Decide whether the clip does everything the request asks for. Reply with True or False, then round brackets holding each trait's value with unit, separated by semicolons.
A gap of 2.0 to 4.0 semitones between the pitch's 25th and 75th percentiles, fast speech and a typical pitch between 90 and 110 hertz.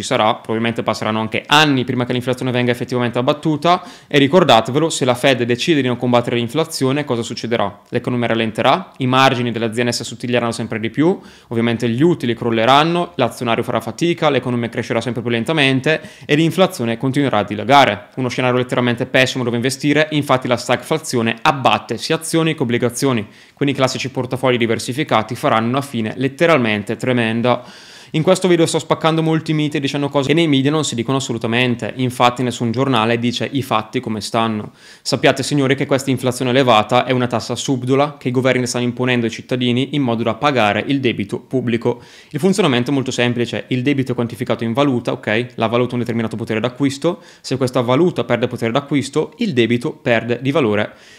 False (3.1 semitones; 180 wpm; 125 Hz)